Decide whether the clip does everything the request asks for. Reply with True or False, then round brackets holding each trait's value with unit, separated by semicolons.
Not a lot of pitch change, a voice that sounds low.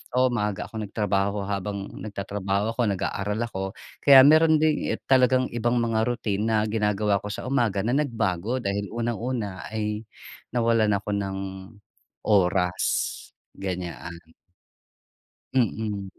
False (3.0 semitones; 105 Hz)